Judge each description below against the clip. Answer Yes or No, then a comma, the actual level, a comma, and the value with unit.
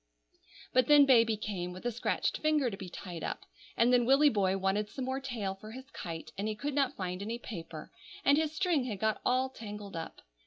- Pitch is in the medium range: No, high, 225 Hz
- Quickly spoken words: Yes, fast, 220 wpm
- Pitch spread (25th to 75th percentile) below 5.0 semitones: No, average, 5.3 semitones